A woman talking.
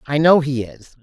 Yes: female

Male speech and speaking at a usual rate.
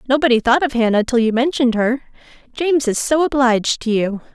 No: female; average, 180 wpm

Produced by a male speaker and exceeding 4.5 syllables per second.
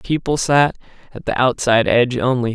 Yes: male; 5.6 syllables/s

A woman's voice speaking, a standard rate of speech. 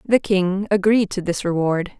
Yes: female; average, 180 wpm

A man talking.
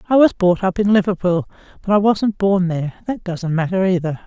No: female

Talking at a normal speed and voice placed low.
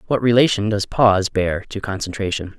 Yes: average, 165 wpm; low, 105 Hz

